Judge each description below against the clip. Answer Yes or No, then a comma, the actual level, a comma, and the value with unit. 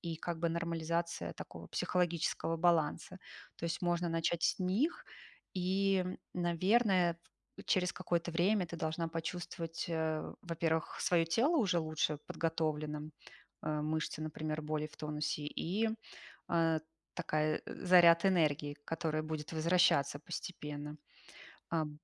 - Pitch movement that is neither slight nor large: No, narrow, 2.1 semitones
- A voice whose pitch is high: No, medium, 165 Hz